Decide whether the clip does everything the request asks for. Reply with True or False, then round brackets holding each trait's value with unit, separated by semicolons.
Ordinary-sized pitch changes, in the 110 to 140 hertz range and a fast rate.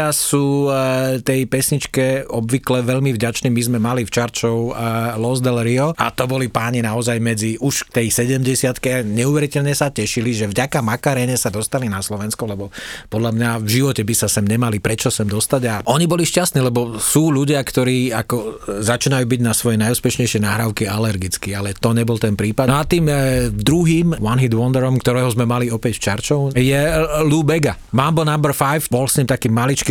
True (3.0 semitones; 125 Hz; 185 wpm)